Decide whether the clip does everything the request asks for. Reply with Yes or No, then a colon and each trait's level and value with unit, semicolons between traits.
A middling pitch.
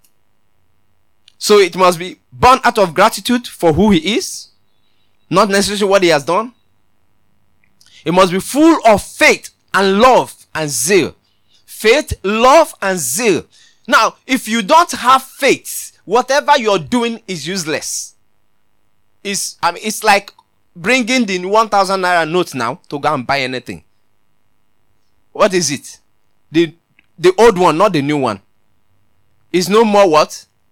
Yes: medium, 170 Hz